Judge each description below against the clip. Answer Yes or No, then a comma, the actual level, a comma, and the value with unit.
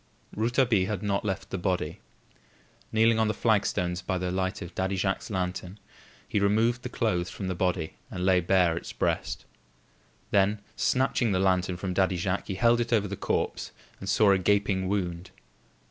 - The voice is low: Yes, very low, 95 Hz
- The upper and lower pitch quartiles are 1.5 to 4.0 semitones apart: Yes, narrow, 2.5 semitones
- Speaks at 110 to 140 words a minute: No, average, 175 wpm